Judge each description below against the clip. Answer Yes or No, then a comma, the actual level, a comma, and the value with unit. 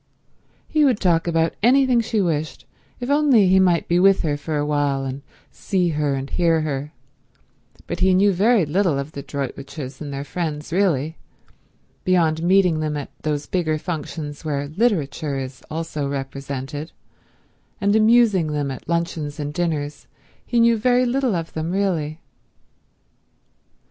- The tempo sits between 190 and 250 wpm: No, average, 150 wpm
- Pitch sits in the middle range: Yes, medium, 160 Hz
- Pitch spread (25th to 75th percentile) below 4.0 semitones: No, average, 4.7 semitones